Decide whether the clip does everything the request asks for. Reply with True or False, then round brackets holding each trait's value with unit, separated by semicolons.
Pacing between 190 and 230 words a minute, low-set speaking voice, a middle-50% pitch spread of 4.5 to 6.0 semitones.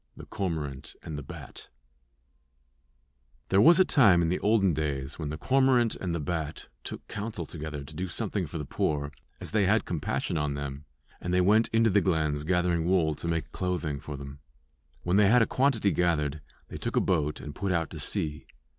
True (200 wpm; 85 Hz; 4.9 semitones)